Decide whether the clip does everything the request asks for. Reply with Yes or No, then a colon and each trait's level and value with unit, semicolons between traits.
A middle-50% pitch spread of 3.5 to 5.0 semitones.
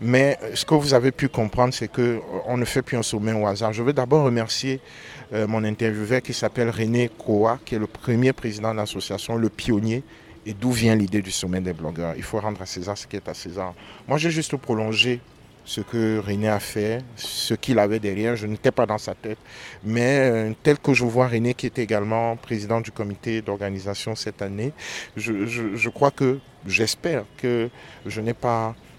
No: average, 2.7 semitones